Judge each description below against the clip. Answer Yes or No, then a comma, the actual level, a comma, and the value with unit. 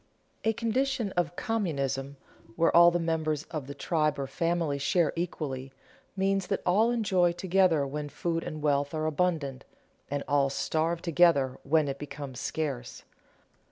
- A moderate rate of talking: Yes, average, 155 wpm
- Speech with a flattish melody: No, average, 3.8 semitones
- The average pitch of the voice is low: No, medium, 160 Hz